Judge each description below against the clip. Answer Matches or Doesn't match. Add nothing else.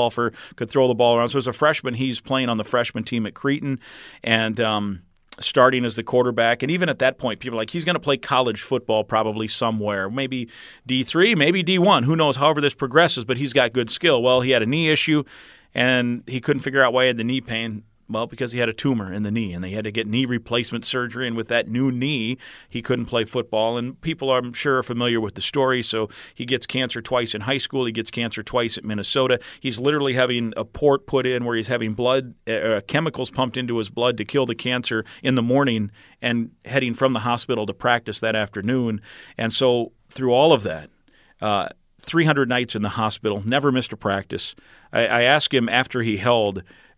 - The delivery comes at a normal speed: Doesn't match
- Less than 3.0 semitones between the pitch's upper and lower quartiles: Matches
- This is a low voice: Matches